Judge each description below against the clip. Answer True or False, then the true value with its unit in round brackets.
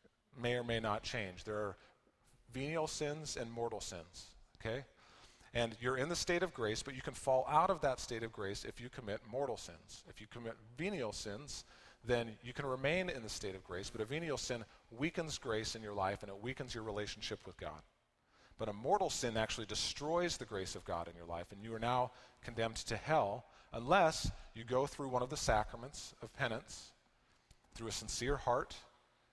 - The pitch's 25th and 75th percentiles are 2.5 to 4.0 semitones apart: True (3.7 semitones)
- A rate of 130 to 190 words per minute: False (205 wpm)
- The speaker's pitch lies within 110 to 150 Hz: True (120 Hz)